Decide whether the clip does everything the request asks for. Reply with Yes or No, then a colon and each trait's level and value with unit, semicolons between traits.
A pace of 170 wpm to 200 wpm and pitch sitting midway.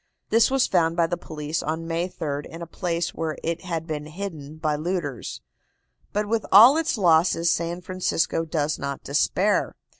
Yes: average, 175 wpm; medium, 165 Hz